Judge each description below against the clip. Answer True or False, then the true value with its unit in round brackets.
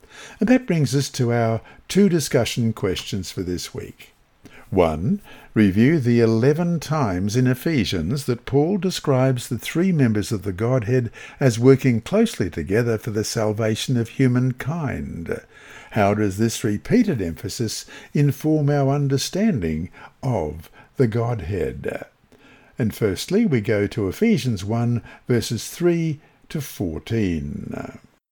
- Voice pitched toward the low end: True (125 Hz)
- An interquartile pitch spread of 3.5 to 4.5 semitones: False (4.9 semitones)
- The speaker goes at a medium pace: False (125 wpm)